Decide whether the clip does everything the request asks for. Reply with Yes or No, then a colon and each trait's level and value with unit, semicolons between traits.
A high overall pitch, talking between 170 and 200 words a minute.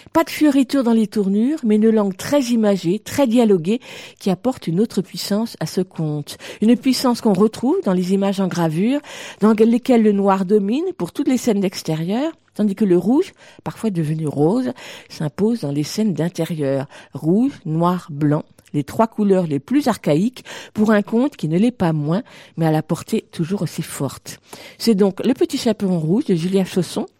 Yes: high, 205 Hz; average, 190 wpm